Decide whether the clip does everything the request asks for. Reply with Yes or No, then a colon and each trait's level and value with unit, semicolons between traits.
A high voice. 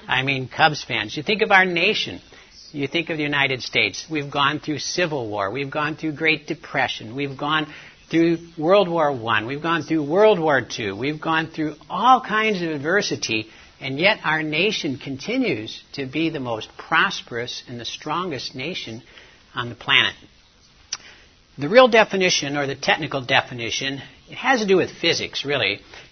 No: medium, 150 Hz